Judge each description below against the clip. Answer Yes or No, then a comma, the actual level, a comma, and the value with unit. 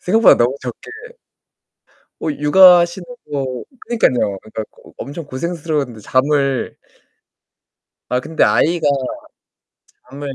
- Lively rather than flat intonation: No, average, 4.7 semitones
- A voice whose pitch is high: No, medium, 145 Hz